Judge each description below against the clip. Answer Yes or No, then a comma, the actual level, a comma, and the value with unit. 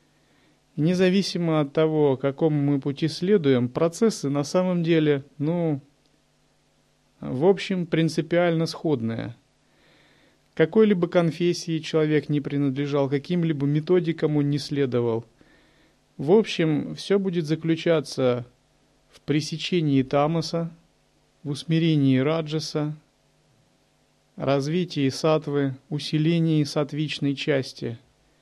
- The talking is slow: Yes, slow, 90 wpm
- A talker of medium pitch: Yes, medium, 155 Hz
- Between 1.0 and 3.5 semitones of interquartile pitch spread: Yes, average, 2.8 semitones